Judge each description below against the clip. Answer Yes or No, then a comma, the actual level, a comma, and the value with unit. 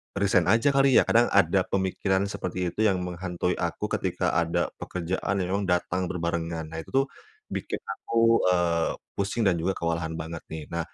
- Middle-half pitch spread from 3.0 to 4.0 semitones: No, narrow, 2.4 semitones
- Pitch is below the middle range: Yes, very low, 90 Hz